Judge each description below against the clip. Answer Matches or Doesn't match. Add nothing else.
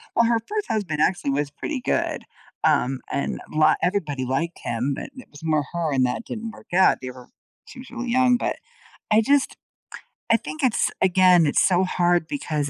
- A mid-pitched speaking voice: Matches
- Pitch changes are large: Matches